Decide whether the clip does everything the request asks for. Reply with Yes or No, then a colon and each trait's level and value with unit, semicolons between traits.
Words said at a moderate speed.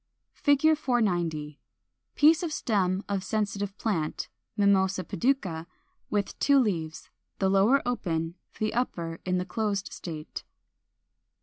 No: slow, 120 wpm